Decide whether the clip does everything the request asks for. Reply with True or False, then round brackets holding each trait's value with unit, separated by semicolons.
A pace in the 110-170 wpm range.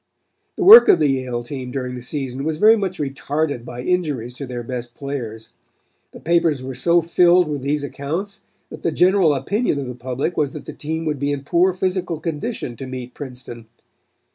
False (195 wpm)